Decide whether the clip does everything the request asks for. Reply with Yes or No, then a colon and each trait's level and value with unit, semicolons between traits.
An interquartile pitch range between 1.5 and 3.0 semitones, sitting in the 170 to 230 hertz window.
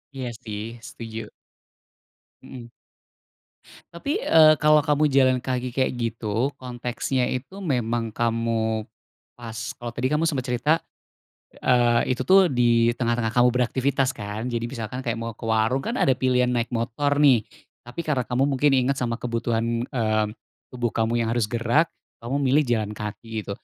No: narrow, 2.5 semitones; low, 120 Hz